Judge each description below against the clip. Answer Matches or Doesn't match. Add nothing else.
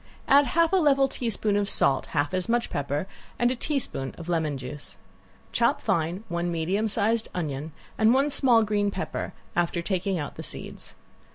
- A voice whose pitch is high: Matches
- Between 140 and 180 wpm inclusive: Matches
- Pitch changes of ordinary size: Doesn't match